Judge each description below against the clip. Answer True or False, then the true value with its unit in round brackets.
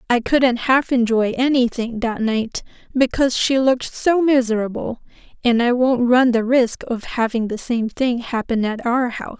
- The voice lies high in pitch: True (240 Hz)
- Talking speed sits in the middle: True (170 wpm)